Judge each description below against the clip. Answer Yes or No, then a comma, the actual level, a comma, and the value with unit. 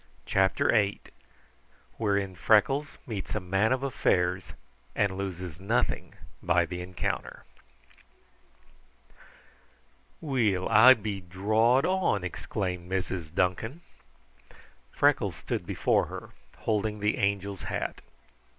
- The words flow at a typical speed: No, slow, 100 wpm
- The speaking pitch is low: Yes, low, 100 Hz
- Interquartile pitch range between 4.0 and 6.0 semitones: No, average, 3.4 semitones